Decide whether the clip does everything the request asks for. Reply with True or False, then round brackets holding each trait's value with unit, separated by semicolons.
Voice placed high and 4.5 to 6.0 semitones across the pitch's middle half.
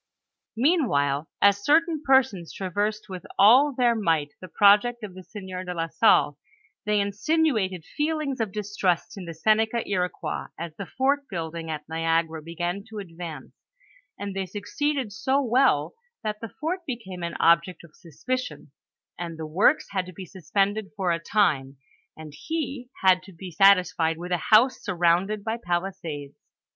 True (195 Hz; 5.0 semitones)